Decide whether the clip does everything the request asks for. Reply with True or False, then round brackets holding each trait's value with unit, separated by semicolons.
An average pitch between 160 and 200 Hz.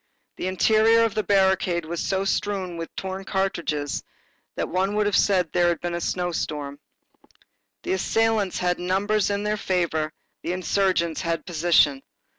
True (185 Hz)